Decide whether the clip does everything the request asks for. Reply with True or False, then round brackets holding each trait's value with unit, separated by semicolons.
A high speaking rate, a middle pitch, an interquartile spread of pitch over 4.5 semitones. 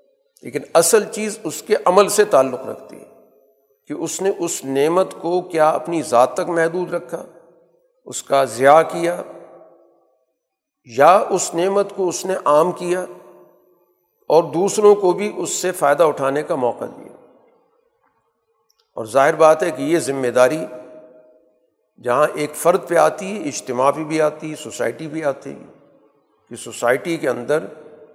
False (150 wpm; 165 Hz; 5.4 semitones)